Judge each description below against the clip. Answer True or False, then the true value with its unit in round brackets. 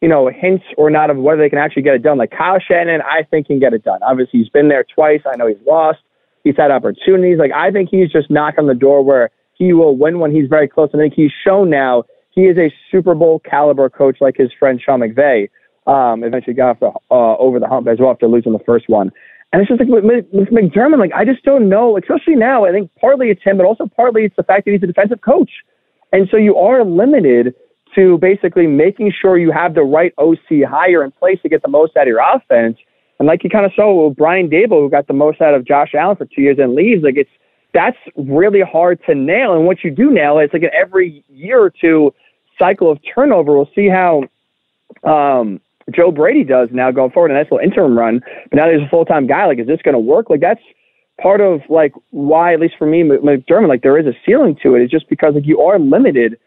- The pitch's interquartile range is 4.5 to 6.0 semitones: True (5.6 semitones)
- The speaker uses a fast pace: True (250 wpm)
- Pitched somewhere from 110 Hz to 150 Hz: False (160 Hz)